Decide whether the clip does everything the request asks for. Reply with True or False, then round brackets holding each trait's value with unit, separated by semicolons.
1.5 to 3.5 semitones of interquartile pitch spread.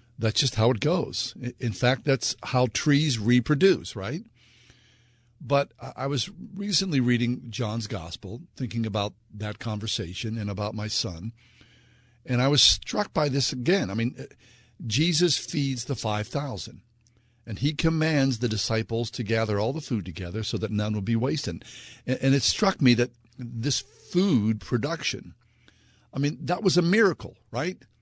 False (3.9 semitones)